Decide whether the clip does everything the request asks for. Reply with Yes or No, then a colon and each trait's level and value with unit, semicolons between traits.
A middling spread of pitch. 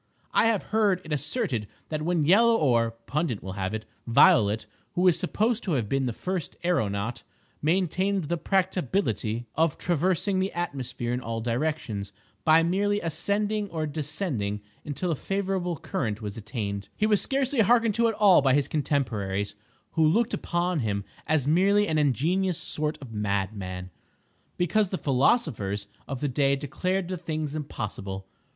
No: wide, 8.3 semitones